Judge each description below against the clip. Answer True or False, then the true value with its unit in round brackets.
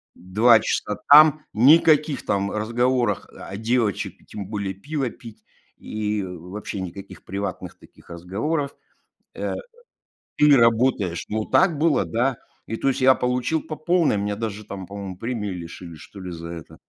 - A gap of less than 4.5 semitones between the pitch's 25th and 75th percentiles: False (5.1 semitones)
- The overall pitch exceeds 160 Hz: False (110 Hz)